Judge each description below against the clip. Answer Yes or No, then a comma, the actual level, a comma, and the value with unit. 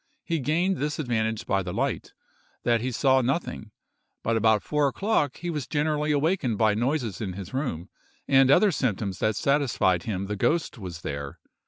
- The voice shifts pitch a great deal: Yes, wide, 6.2 semitones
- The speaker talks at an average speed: Yes, average, 175 wpm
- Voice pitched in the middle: No, low, 125 Hz